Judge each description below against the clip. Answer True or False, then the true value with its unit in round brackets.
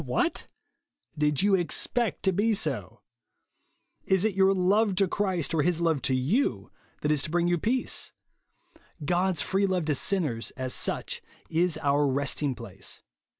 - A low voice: False (175 Hz)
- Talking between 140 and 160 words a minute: True (155 wpm)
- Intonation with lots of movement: False (4.8 semitones)